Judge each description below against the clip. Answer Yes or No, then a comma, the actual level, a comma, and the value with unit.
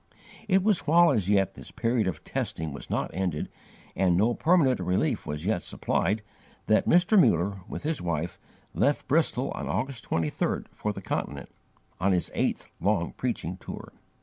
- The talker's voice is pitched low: Yes, low, 100 Hz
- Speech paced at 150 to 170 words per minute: Yes, average, 165 wpm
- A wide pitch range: Yes, wide, 7.1 semitones